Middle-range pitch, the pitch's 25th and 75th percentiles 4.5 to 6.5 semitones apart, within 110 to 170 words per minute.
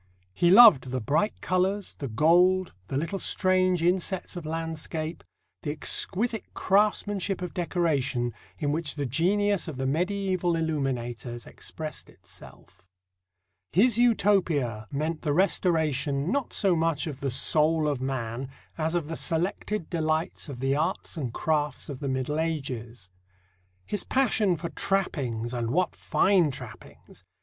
Yes: medium, 160 Hz; average, 5.0 semitones; average, 140 wpm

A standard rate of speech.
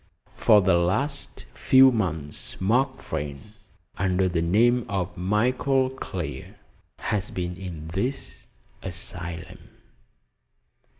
No: slow, 100 wpm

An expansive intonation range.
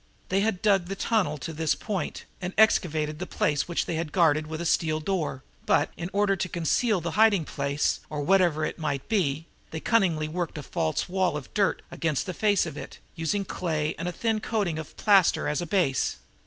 No: average, 4.1 semitones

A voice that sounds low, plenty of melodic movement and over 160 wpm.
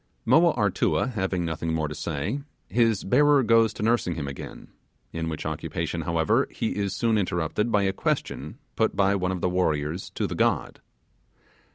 Yes: very low, 95 Hz; wide, 5.7 semitones; average, 175 wpm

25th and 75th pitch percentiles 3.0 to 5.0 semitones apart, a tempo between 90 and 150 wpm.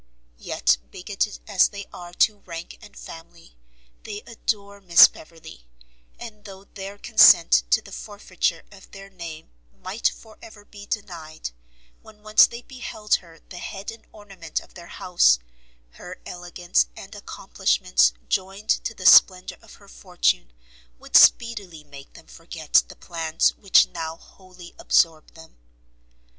Yes: average, 3.8 semitones; average, 140 wpm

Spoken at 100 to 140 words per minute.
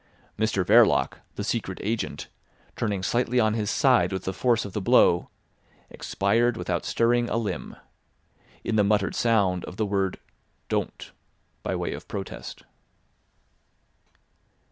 Yes: slow, 135 wpm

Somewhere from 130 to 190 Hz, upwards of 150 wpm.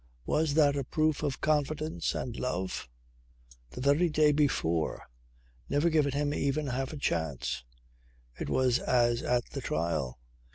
No: medium, 140 Hz; average, 140 wpm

